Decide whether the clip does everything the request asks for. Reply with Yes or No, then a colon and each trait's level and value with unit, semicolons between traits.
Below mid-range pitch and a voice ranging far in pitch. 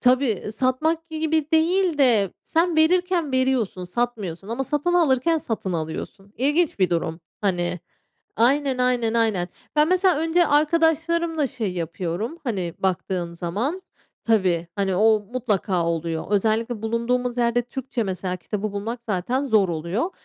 No: high, 235 Hz; wide, 7.6 semitones